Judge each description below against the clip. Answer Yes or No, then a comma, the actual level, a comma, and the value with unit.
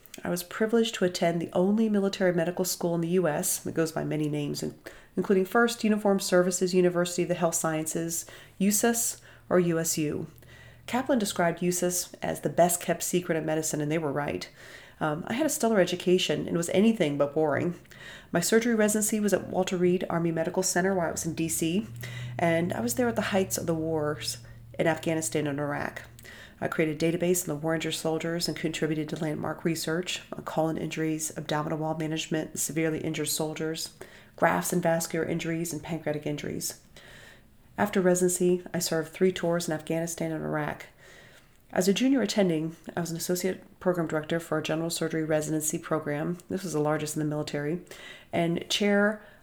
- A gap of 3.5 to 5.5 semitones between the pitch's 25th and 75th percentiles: No, narrow, 2.5 semitones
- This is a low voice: No, medium, 165 Hz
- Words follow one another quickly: No, average, 180 wpm